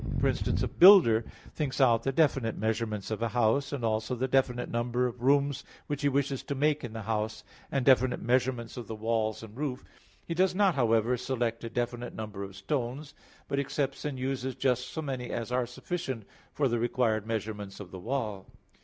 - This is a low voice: Yes, low, 125 Hz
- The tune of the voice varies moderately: Yes, average, 3.4 semitones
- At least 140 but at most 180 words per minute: No, average, 200 wpm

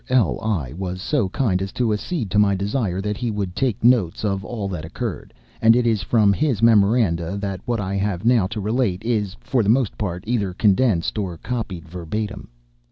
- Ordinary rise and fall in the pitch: Yes, average, 3.6 semitones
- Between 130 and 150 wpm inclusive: No, average, 195 wpm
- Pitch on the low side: Yes, low, 105 Hz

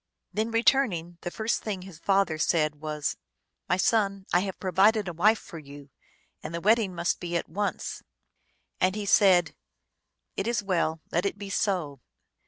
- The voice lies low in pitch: No, medium, 185 Hz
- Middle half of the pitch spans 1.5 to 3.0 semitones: No, average, 3.6 semitones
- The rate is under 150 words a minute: No, average, 180 wpm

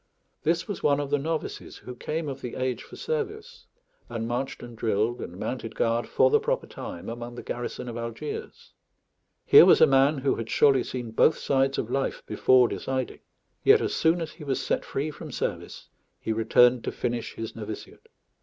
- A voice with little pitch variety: No, average, 3.7 semitones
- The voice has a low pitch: Yes, low, 130 Hz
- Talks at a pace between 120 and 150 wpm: No, average, 190 wpm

